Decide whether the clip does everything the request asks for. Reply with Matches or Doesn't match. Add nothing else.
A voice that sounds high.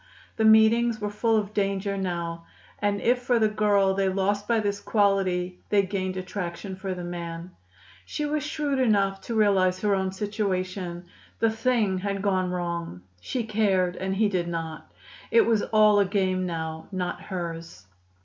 Matches